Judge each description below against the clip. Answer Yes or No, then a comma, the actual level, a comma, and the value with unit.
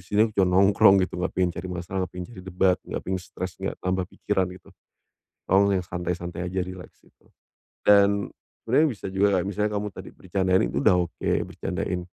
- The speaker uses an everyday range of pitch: No, narrow, 1.7 semitones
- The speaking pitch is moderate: No, very low, 95 Hz